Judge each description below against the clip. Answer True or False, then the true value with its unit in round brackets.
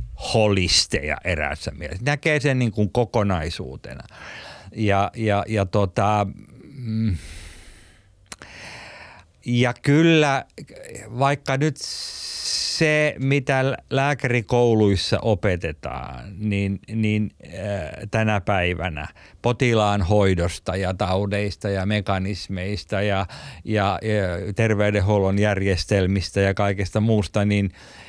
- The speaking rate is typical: False (85 wpm)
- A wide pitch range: False (2.8 semitones)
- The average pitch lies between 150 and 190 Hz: False (105 Hz)